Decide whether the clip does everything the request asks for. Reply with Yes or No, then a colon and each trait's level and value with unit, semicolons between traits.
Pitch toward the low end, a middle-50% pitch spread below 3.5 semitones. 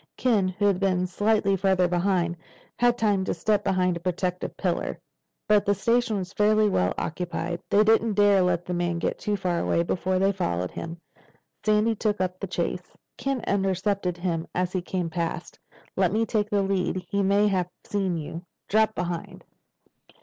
No: high, 190 Hz; narrow, 2.6 semitones